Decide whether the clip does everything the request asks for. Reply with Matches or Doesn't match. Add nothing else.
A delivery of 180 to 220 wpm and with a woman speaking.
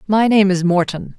Matches